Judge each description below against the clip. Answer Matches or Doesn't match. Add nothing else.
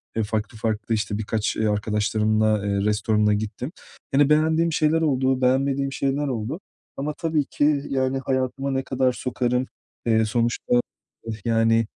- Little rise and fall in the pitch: Doesn't match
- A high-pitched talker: Doesn't match